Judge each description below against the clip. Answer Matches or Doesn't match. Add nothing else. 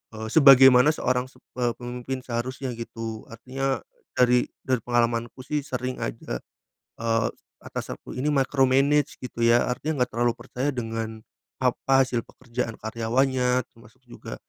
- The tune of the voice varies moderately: Doesn't match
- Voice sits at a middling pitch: Doesn't match